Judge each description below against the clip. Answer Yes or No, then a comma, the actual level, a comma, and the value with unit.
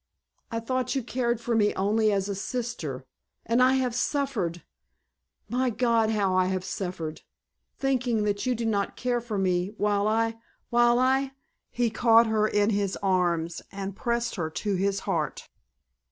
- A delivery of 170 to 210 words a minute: No, average, 155 wpm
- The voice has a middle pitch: No, high, 220 Hz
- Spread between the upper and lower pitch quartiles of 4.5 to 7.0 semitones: No, average, 3.5 semitones